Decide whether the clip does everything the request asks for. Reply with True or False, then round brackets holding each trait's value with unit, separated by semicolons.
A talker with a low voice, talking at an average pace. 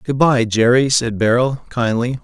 True (125 Hz; 160 wpm)